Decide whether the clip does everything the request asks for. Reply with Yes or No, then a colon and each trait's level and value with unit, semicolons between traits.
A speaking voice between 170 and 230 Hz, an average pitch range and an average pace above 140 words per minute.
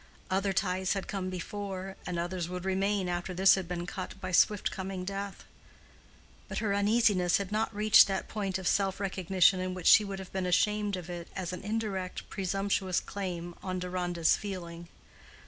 No: high, 190 Hz; narrow, 1.7 semitones; average, 180 wpm